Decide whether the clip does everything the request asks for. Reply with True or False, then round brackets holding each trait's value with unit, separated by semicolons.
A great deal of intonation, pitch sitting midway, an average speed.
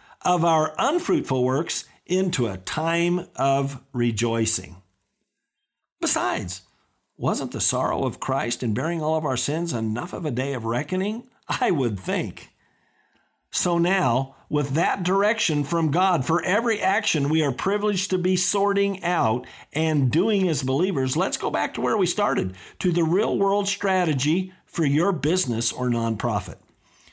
True (6.6 semitones; 160 Hz; 150 wpm)